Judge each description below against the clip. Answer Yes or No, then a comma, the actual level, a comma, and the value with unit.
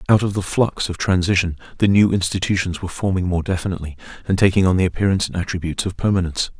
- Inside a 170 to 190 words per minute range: No, average, 200 wpm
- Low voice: Yes, very low, 90 Hz